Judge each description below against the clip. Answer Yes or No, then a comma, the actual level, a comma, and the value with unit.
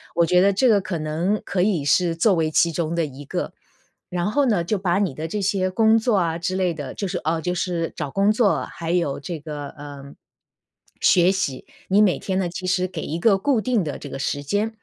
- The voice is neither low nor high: Yes, medium, 180 Hz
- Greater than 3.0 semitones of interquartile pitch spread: Yes, average, 3.9 semitones